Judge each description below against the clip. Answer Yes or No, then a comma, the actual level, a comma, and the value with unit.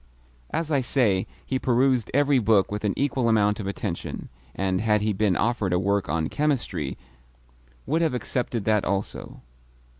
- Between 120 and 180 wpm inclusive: Yes, average, 160 wpm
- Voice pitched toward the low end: Yes, low, 110 Hz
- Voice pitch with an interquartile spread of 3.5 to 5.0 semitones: Yes, average, 4.7 semitones